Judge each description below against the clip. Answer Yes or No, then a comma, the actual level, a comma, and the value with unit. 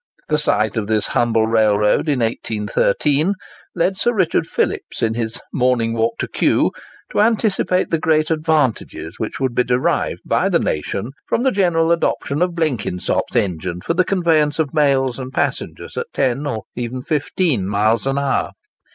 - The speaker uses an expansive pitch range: Yes, wide, 6.3 semitones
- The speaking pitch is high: No, low, 135 Hz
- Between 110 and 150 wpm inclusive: No, average, 165 wpm